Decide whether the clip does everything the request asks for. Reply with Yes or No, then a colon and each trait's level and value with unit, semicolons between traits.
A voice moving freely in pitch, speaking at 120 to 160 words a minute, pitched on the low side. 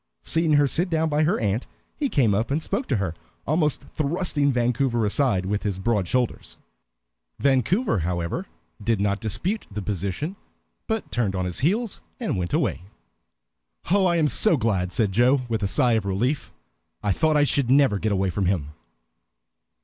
No: wide, 7.3 semitones; average, 175 wpm; low, 120 Hz